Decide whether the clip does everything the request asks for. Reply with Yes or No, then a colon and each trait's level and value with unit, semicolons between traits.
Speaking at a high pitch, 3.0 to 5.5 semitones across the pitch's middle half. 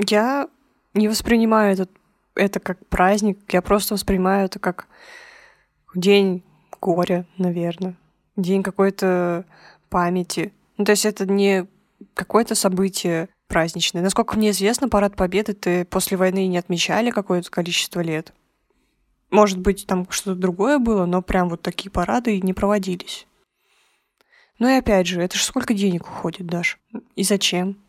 No: high, 195 Hz; narrow, 2.6 semitones